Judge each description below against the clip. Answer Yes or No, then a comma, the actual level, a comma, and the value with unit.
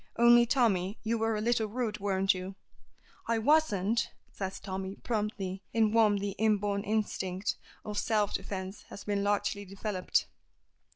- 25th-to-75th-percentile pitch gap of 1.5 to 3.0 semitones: Yes, narrow, 2.5 semitones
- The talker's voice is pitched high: Yes, high, 205 Hz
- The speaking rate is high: No, average, 140 wpm